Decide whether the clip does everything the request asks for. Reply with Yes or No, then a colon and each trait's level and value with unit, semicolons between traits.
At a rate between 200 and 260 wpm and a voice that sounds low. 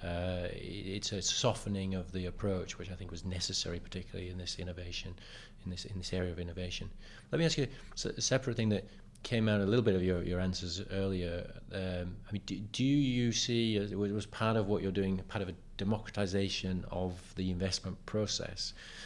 Yes: fast, 205 wpm; very low, 95 Hz